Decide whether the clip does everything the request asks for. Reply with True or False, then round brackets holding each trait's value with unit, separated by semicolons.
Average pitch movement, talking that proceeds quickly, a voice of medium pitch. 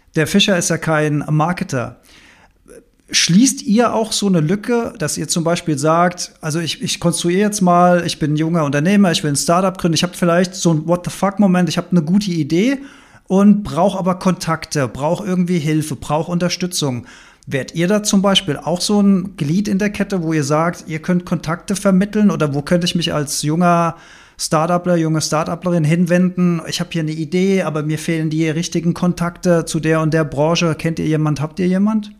True (3.0 semitones; 200 wpm; 175 Hz)